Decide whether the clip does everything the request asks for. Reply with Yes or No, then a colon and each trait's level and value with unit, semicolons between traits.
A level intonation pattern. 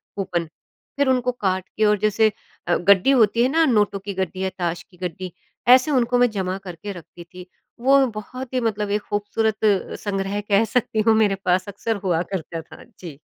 No: average, 3.7 semitones